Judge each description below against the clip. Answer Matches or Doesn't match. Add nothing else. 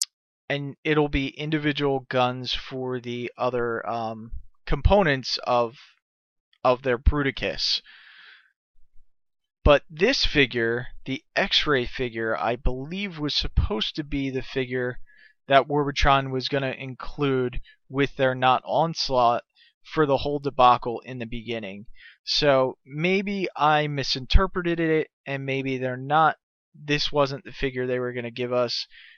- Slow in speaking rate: Matches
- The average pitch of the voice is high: Doesn't match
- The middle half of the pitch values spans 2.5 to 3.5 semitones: Matches